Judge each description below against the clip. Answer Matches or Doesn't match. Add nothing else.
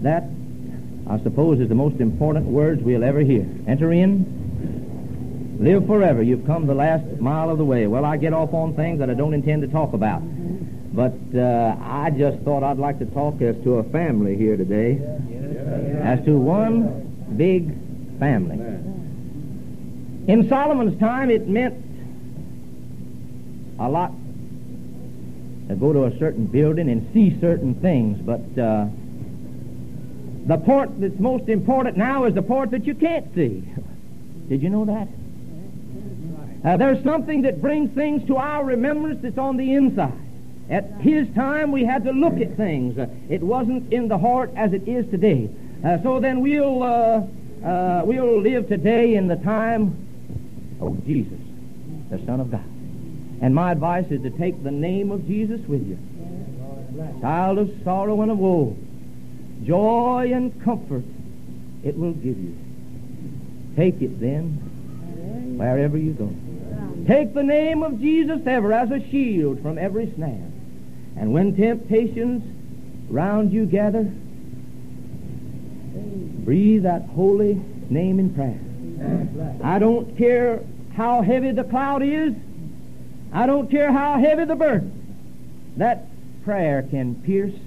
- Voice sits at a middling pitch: Matches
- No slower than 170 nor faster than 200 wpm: Doesn't match